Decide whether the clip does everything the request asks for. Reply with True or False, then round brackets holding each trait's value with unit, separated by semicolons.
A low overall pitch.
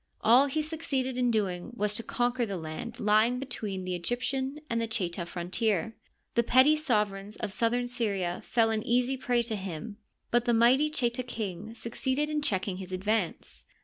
False (230 Hz)